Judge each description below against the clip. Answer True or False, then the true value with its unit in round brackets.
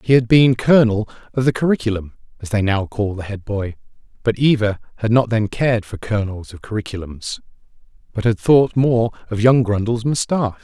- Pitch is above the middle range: False (110 Hz)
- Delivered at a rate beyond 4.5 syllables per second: True (5.7 syllables/s)